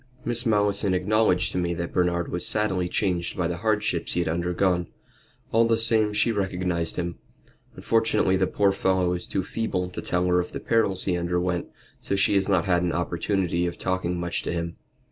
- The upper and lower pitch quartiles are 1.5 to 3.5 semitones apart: Yes, narrow, 2.6 semitones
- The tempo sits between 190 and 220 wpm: Yes, average, 195 wpm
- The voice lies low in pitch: Yes, very low, 90 Hz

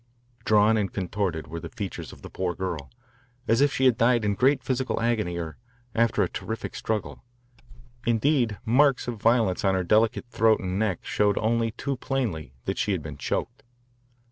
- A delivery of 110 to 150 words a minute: No, average, 180 wpm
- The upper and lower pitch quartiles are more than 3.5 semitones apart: Yes, average, 3.9 semitones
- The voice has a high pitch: No, low, 110 Hz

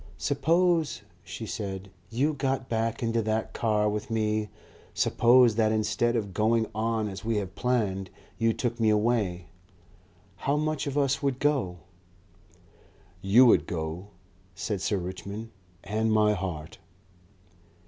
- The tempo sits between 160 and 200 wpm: No, slow, 135 wpm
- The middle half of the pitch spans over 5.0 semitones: No, average, 3.4 semitones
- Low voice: Yes, low, 110 Hz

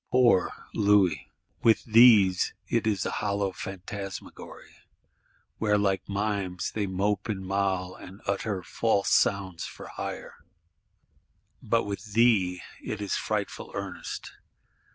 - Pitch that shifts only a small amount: Yes, narrow, 2.2 semitones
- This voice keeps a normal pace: No, slow, 115 wpm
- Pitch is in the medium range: No, low, 100 Hz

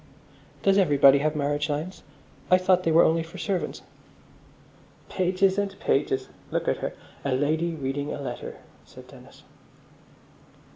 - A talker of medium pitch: Yes, medium, 165 Hz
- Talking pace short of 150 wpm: Yes, average, 140 wpm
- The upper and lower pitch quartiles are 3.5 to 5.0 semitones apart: Yes, average, 4.5 semitones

